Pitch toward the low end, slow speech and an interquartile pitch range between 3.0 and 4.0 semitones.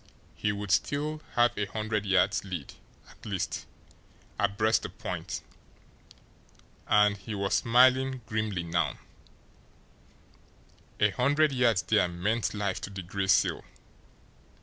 Yes: low, 105 Hz; slow, 120 wpm; average, 3.4 semitones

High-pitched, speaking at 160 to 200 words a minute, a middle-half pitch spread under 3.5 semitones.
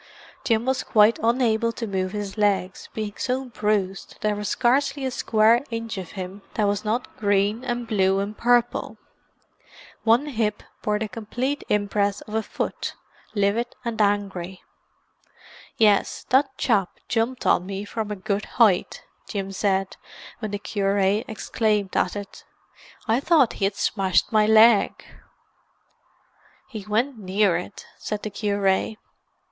No: high, 210 Hz; average, 145 wpm; narrow, 2.5 semitones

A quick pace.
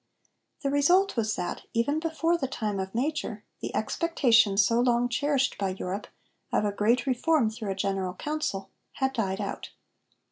No: average, 165 wpm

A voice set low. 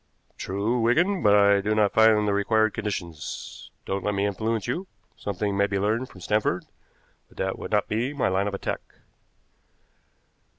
Yes: low, 105 Hz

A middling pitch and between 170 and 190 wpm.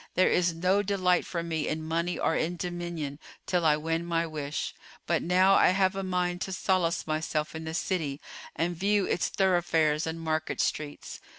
Yes: medium, 170 Hz; average, 185 wpm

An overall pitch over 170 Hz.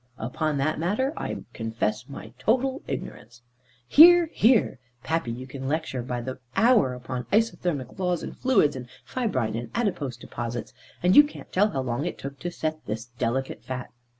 No: medium, 140 Hz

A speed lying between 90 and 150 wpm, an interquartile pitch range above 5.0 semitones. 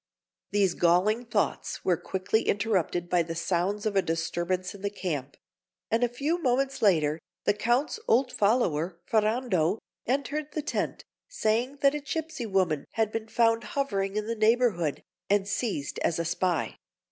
No: average, 160 wpm; wide, 5.4 semitones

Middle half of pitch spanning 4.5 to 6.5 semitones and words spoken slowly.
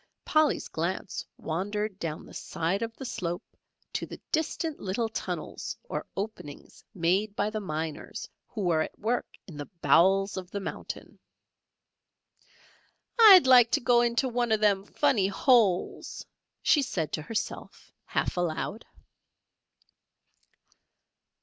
Yes: average, 5.2 semitones; slow, 130 wpm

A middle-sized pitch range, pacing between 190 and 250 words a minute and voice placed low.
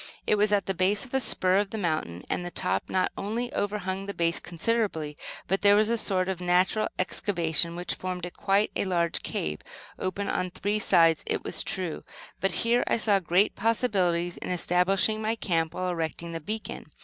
No: average, 3.2 semitones; average, 195 wpm; medium, 185 Hz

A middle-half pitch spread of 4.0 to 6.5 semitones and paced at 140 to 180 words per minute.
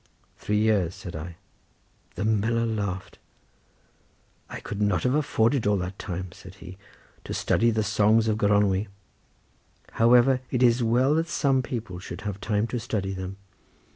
No: average, 3.2 semitones; average, 155 wpm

